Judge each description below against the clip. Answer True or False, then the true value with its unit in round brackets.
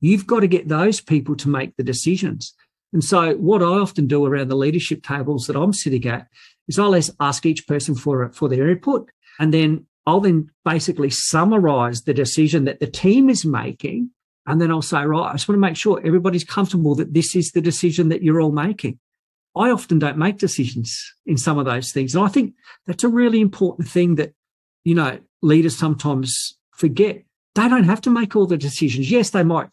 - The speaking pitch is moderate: True (160 Hz)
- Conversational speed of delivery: False (210 wpm)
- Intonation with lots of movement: False (4.7 semitones)